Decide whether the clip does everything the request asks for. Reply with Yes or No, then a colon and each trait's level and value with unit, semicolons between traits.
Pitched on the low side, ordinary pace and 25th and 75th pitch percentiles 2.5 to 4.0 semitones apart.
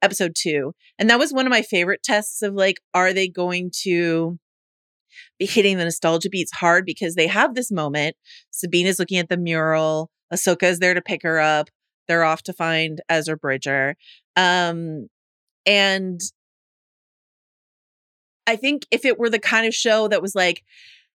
No: medium, 180 Hz; average, 170 wpm; average, 3.5 semitones